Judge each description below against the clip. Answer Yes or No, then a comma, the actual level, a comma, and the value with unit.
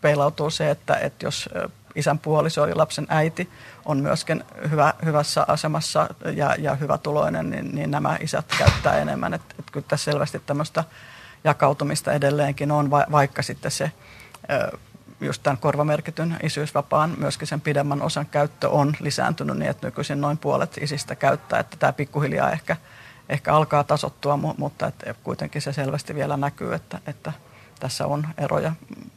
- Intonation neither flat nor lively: No, narrow, 1.3 semitones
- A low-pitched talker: No, medium, 145 Hz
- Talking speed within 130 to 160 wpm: Yes, average, 150 wpm